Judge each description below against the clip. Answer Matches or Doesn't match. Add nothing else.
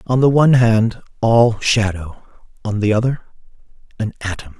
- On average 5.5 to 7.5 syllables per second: Doesn't match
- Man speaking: Matches